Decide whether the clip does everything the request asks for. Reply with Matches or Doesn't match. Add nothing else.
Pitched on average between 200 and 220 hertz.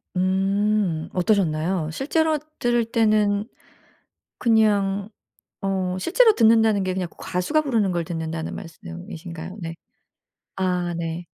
Doesn't match